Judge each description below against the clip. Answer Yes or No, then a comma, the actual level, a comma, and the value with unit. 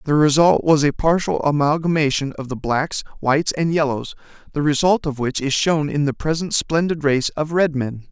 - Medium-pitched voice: Yes, medium, 150 Hz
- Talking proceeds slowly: No, average, 190 wpm